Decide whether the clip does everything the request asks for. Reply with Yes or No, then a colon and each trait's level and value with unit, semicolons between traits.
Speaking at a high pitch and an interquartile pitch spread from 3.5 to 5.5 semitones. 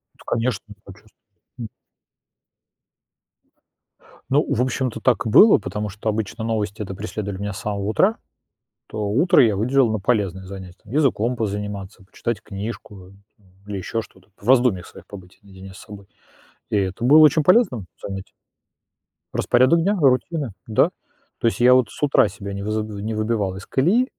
No: low, 110 Hz; average, 4.2 semitones